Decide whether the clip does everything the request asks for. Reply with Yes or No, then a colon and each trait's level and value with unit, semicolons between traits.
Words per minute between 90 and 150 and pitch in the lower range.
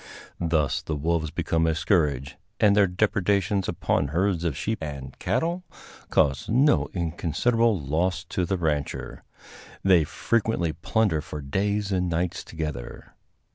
Yes: slow, 135 wpm; very low, 85 Hz